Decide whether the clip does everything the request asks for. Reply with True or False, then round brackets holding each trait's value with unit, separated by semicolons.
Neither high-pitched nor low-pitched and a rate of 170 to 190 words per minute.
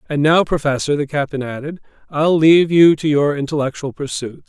True (150 Hz; 175 wpm)